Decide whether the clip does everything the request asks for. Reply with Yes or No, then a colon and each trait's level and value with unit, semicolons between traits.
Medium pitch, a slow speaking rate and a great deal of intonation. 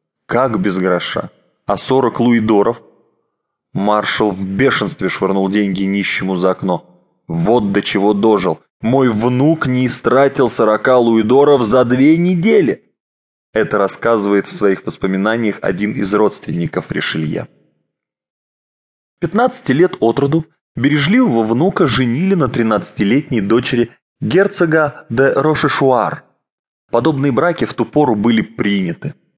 No: low, 115 Hz; slow, 115 wpm; wide, 5.8 semitones